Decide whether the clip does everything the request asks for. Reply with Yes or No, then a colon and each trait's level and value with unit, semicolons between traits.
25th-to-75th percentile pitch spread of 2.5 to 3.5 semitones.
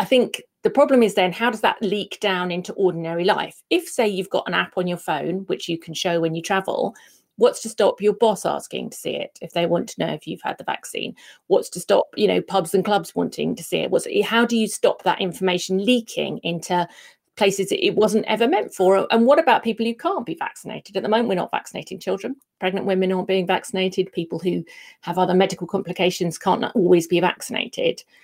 No: average, 4.2 semitones